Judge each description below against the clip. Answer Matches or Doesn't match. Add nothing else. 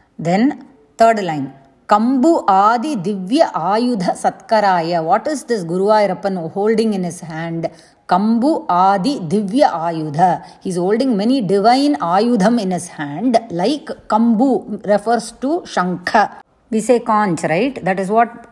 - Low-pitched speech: Doesn't match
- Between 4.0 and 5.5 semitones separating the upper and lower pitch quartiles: Matches